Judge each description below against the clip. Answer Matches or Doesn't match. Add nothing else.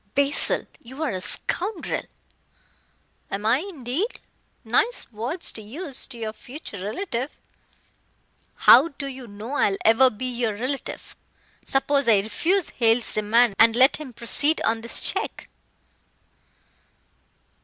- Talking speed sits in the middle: Doesn't match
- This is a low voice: Doesn't match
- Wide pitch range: Doesn't match